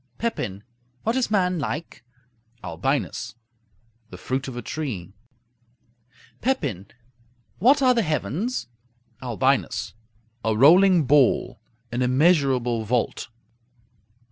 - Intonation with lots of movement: Yes, wide, 7.7 semitones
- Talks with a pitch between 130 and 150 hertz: Yes, low, 135 Hz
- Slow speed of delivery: Yes, slow, 95 wpm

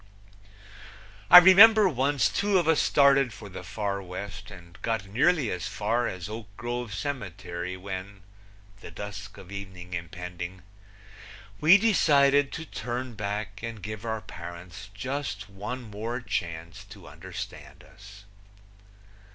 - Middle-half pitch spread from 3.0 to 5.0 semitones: No, wide, 5.5 semitones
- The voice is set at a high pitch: No, low, 105 Hz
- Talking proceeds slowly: Yes, slow, 130 wpm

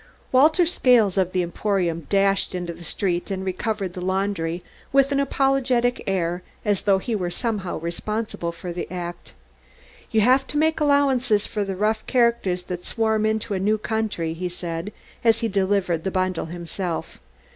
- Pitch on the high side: Yes, high, 195 Hz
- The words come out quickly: No, average, 165 wpm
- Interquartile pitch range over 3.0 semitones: Yes, average, 4.3 semitones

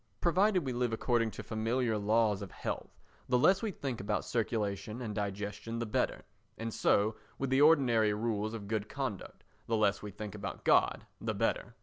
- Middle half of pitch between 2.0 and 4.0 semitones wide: Yes, average, 3.0 semitones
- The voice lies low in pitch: Yes, low, 110 Hz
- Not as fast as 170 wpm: No, average, 185 wpm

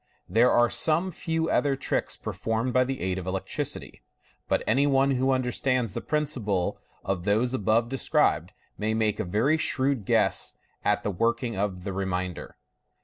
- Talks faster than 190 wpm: No, average, 160 wpm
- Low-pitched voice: Yes, low, 115 Hz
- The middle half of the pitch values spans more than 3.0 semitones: Yes, average, 5.1 semitones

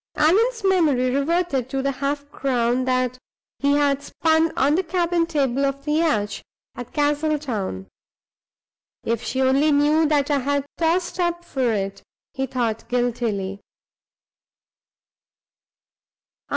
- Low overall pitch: No, very high, 280 Hz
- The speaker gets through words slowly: Yes, slow, 125 wpm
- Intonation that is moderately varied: Yes, average, 4.0 semitones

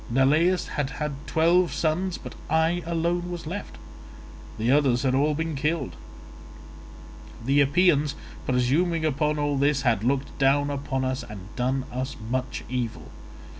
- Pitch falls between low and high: Yes, medium, 145 Hz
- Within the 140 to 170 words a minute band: Yes, average, 145 wpm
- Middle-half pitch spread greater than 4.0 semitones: No, average, 3.7 semitones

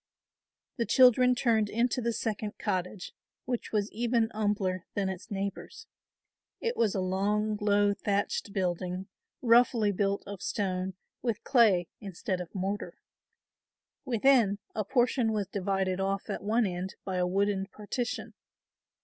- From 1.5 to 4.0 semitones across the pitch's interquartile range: Yes, average, 3.1 semitones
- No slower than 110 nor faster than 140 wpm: Yes, slow, 135 wpm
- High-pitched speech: Yes, high, 205 Hz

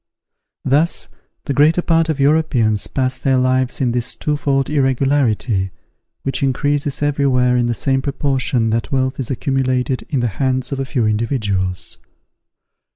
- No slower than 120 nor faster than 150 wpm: Yes, average, 145 wpm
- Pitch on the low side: Yes, low, 130 Hz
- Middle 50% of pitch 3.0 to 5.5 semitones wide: No, narrow, 2.5 semitones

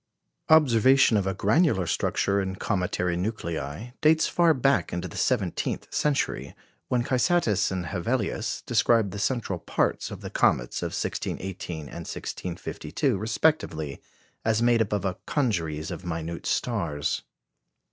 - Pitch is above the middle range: No, low, 100 Hz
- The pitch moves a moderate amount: No, wide, 5.7 semitones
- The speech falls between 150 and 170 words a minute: No, slow, 135 wpm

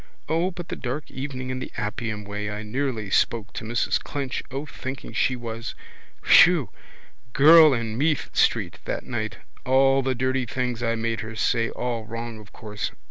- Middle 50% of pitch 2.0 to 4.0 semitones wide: Yes, average, 3.2 semitones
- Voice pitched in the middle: No, low, 125 Hz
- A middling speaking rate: Yes, average, 175 wpm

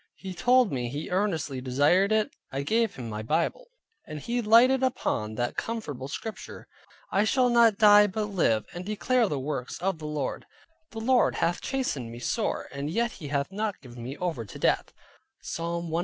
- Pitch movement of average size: No, wide, 8.0 semitones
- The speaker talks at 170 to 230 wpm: Yes, average, 185 wpm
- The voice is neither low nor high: Yes, medium, 180 Hz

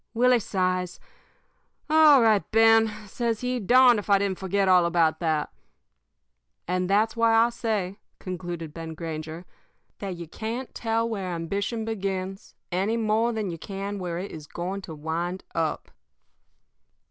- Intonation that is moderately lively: Yes, average, 4.3 semitones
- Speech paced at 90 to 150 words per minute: Yes, average, 145 wpm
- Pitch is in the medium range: No, high, 195 Hz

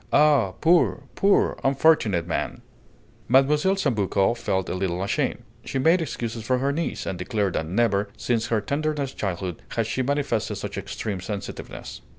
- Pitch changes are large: Yes, wide, 6.4 semitones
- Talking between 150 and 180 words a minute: Yes, average, 155 wpm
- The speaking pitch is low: Yes, low, 115 Hz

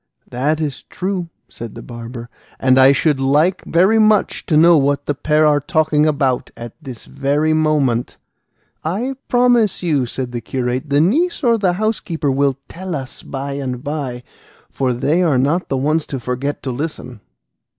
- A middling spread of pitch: Yes, average, 4.3 semitones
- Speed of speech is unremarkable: Yes, average, 170 wpm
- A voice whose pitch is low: No, medium, 145 Hz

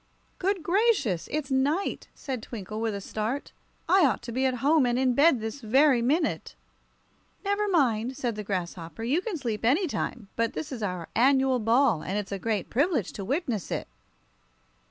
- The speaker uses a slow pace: No, average, 180 wpm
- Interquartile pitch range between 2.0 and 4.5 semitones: No, average, 5.2 semitones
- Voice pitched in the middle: No, very high, 250 Hz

